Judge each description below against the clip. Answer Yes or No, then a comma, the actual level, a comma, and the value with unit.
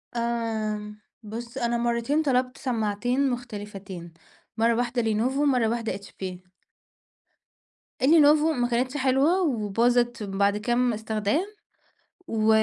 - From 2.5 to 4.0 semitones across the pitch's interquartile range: Yes, average, 3.1 semitones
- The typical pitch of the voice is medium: No, high, 235 Hz